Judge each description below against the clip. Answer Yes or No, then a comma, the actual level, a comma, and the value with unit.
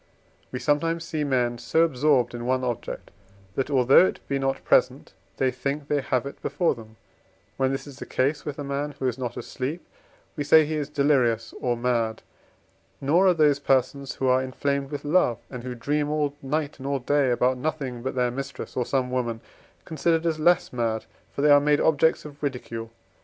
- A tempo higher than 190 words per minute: Yes, average, 200 wpm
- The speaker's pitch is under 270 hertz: Yes, medium, 140 Hz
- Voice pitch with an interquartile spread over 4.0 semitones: No, average, 2.7 semitones